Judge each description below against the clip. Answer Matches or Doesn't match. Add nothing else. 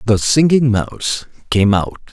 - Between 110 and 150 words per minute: Matches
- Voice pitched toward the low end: Matches